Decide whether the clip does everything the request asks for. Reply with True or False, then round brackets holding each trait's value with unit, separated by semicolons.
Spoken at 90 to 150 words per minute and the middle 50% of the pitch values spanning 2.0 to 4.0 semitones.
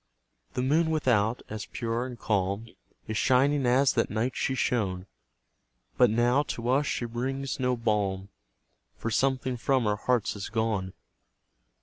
True (145 wpm; 3.2 semitones)